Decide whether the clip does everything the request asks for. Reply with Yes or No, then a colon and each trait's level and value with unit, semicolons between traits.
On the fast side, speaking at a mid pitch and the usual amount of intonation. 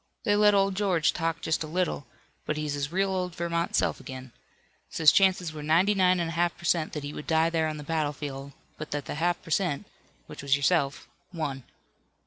Yes: fast, 215 wpm; medium, 165 Hz; average, 3.4 semitones